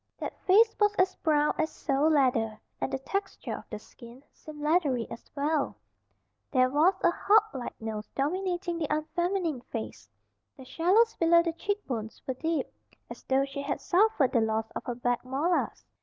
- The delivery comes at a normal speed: Yes, average, 170 wpm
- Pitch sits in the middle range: No, very high, 300 Hz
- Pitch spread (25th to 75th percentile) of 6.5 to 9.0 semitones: No, wide, 5.6 semitones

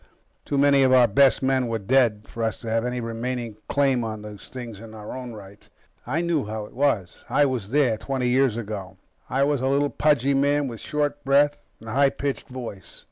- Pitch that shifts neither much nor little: Yes, average, 3.8 semitones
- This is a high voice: No, low, 125 Hz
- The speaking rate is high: Yes, fast, 215 wpm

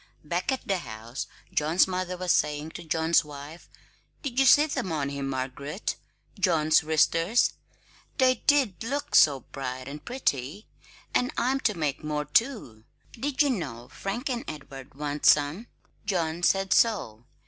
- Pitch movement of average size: No, wide, 7.8 semitones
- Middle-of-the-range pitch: Yes, medium, 165 Hz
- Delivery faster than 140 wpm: Yes, average, 150 wpm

